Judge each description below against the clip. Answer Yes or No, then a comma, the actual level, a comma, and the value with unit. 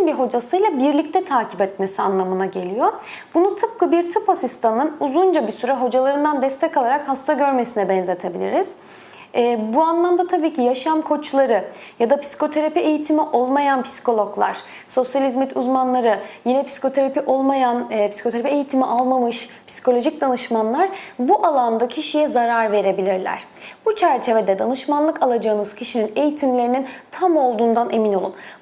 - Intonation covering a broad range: No, average, 4.5 semitones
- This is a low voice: No, very high, 265 Hz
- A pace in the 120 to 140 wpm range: Yes, average, 125 wpm